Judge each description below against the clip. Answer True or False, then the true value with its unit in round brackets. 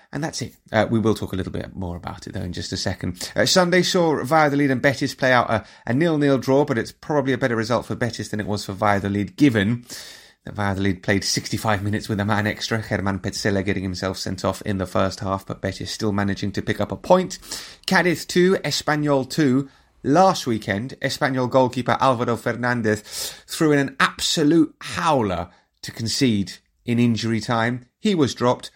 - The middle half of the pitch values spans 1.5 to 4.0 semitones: False (5.3 semitones)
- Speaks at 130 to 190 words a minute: False (200 wpm)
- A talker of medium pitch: False (115 Hz)